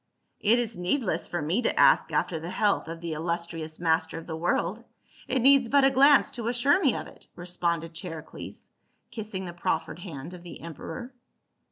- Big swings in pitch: Yes, wide, 6.2 semitones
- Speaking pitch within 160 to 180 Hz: Yes, medium, 175 Hz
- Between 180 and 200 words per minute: Yes, average, 190 wpm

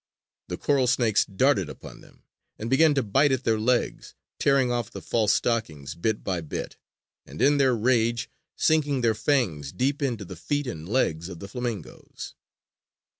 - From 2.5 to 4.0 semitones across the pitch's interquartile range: No, average, 4.7 semitones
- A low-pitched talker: Yes, low, 120 Hz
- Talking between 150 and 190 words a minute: Yes, average, 170 wpm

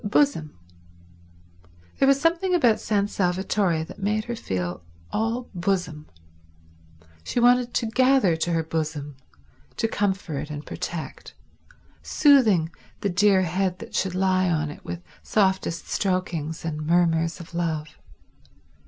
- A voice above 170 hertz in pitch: Yes, medium, 185 Hz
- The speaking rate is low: Yes, slow, 125 wpm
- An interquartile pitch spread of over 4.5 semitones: Yes, average, 4.9 semitones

